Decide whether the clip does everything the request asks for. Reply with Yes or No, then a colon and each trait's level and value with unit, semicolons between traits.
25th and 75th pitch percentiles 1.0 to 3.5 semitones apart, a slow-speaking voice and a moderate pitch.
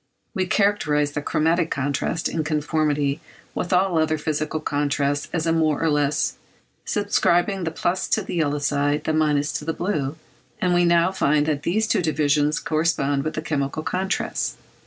No: average, 2.7 semitones; average, 170 wpm; medium, 155 Hz